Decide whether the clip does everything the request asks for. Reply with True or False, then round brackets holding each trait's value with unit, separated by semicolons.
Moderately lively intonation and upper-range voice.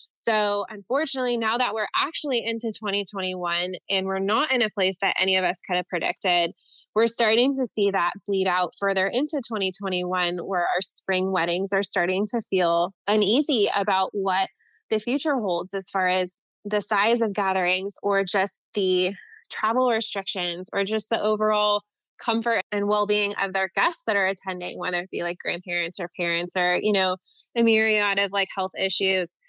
True (3.0 semitones; 195 Hz)